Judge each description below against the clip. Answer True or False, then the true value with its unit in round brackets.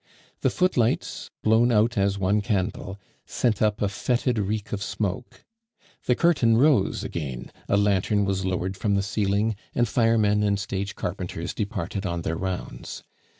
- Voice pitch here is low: True (100 Hz)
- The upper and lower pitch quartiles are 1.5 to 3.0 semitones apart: True (2.6 semitones)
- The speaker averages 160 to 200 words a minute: False (150 wpm)